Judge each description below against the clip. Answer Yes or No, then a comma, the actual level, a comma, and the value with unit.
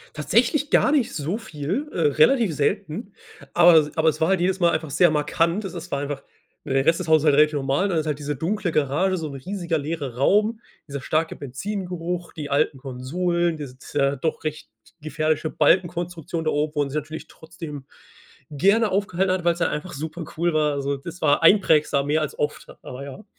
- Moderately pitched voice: Yes, medium, 160 Hz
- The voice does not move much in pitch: No, average, 3.5 semitones